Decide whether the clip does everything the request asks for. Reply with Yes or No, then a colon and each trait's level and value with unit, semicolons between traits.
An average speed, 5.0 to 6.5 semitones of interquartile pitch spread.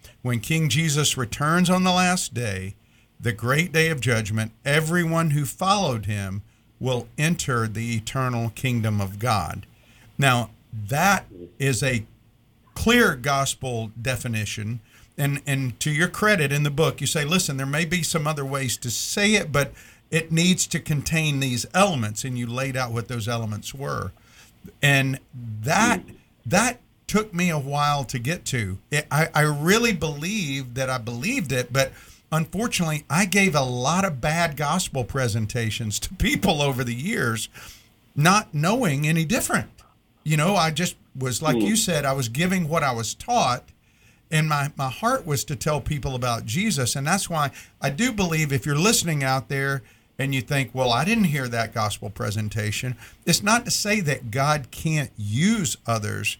Yes: average, 170 wpm; wide, 5.6 semitones